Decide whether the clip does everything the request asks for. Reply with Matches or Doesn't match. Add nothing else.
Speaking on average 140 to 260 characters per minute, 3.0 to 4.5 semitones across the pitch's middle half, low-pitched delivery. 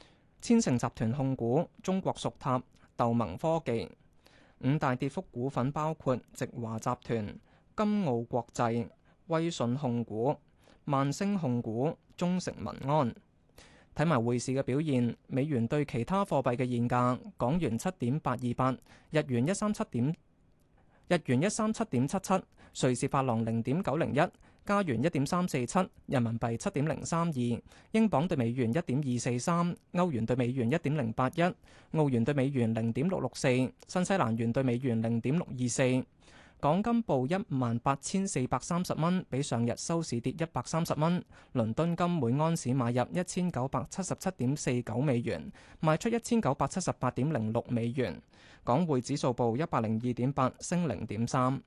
Doesn't match